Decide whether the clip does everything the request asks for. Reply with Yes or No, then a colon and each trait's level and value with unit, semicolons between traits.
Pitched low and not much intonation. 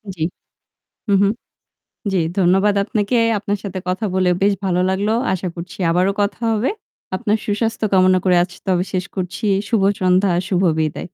No: high, 190 Hz; narrow, 2.1 semitones